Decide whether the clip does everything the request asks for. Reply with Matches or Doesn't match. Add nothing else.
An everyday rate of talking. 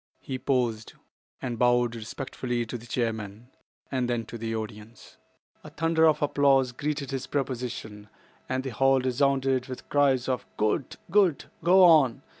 Matches